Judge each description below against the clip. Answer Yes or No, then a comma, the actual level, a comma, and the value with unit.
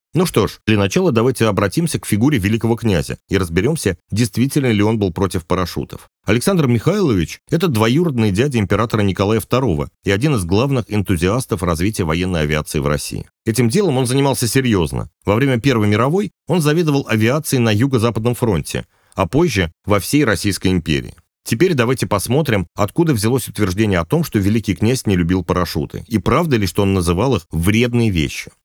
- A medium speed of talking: No, fast, 170 wpm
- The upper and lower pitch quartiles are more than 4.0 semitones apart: Yes, average, 5.0 semitones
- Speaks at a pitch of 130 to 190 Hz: No, low, 110 Hz